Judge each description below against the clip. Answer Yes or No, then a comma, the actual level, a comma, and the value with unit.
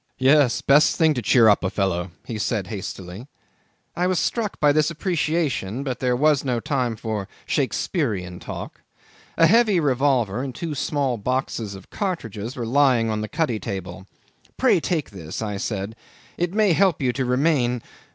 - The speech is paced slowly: No, average, 170 wpm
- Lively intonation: Yes, wide, 6.0 semitones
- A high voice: No, low, 125 Hz